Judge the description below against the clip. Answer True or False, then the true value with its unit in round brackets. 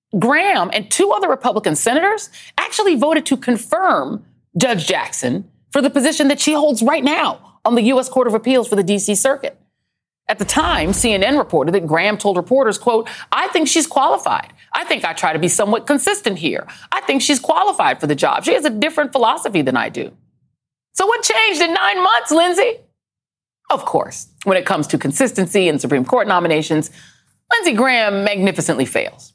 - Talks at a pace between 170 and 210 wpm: True (185 wpm)